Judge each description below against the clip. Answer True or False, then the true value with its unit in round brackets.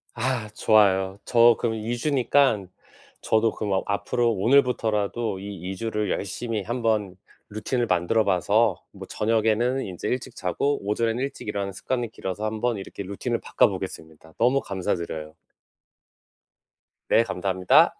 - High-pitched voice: False (110 Hz)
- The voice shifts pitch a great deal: False (3.5 semitones)